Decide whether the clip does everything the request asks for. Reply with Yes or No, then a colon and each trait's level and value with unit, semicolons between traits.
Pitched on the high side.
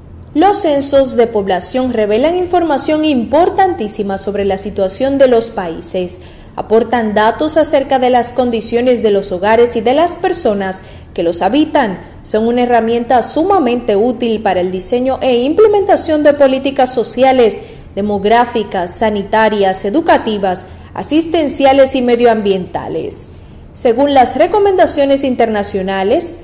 Yes: high, 245 Hz